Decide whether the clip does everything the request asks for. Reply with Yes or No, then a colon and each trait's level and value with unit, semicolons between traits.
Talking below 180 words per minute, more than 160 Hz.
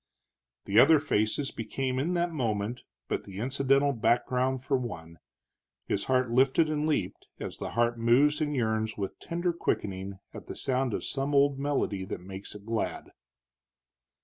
No: average, 160 wpm; low, 125 Hz